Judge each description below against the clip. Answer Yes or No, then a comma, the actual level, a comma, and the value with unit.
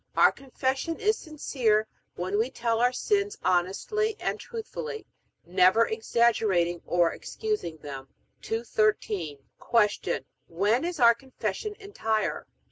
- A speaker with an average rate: No, slow, 115 wpm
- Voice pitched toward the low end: No, high, 230 Hz